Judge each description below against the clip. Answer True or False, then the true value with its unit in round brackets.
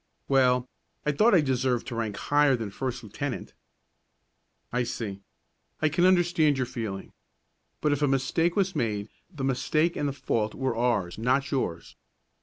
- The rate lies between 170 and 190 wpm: False (160 wpm)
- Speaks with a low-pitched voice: True (130 Hz)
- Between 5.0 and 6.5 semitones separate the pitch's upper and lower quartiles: False (4.2 semitones)